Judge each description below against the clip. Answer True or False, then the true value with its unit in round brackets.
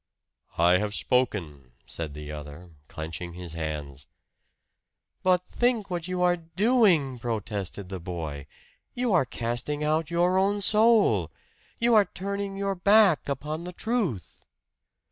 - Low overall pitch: False (150 Hz)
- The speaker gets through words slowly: True (130 wpm)